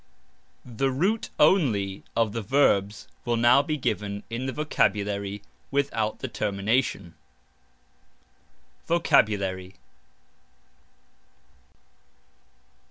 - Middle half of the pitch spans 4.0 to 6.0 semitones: Yes, average, 5.2 semitones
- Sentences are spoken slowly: Yes, slow, 80 wpm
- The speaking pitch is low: Yes, low, 115 Hz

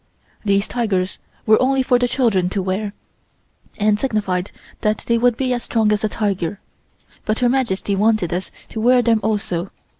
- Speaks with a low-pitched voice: No, high, 215 Hz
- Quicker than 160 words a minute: Yes, average, 175 wpm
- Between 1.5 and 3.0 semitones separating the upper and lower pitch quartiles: No, average, 3.4 semitones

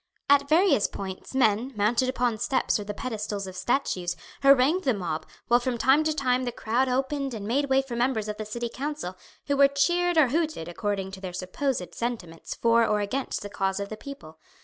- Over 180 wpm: Yes, fast, 205 wpm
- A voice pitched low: No, high, 240 Hz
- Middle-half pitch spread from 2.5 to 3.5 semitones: No, average, 5.2 semitones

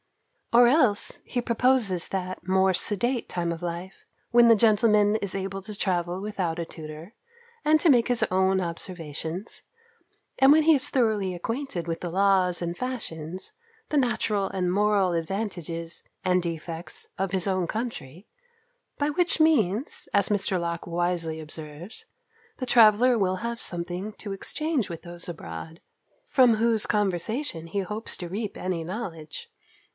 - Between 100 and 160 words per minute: Yes, average, 150 wpm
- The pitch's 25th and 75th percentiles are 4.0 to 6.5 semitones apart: Yes, average, 4.8 semitones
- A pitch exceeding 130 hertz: Yes, high, 190 Hz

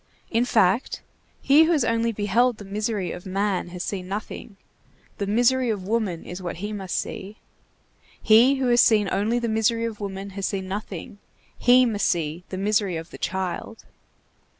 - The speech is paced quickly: No, average, 175 wpm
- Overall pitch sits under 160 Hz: No, high, 205 Hz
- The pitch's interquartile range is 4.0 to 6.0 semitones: No, average, 3.4 semitones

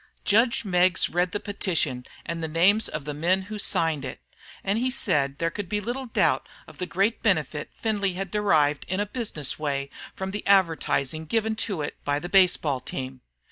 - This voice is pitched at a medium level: Yes, medium, 180 Hz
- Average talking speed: Yes, average, 190 wpm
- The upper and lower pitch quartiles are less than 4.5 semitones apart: No, average, 5.3 semitones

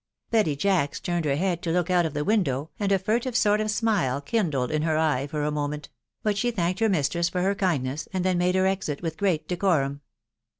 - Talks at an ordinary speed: No, fast, 225 wpm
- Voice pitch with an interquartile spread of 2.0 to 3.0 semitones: No, average, 4.9 semitones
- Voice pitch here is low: No, medium, 175 Hz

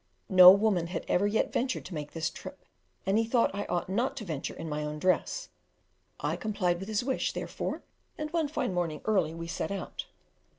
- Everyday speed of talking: No, fast, 210 wpm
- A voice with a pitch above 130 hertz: Yes, high, 190 Hz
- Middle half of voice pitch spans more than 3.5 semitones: Yes, average, 4.7 semitones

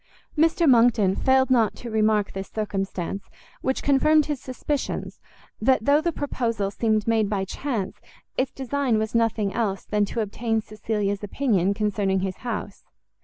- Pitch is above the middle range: Yes, high, 220 Hz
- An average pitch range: Yes, average, 4.3 semitones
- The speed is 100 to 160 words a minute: Yes, average, 150 wpm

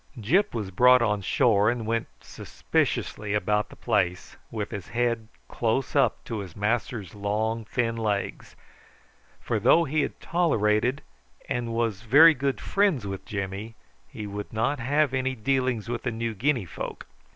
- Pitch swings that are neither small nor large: Yes, average, 3.6 semitones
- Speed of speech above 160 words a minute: No, average, 155 wpm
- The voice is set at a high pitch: No, low, 115 Hz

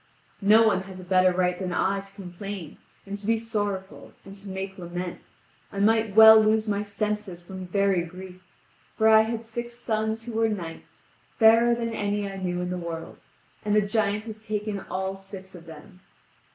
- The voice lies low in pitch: No, high, 200 Hz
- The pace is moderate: Yes, average, 190 wpm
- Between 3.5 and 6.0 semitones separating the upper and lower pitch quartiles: No, average, 2.9 semitones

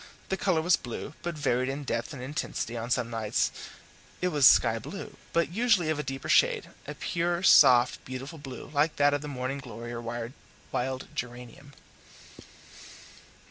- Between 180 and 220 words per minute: No, average, 165 wpm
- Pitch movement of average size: Yes, average, 4.1 semitones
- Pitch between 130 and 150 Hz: Yes, low, 135 Hz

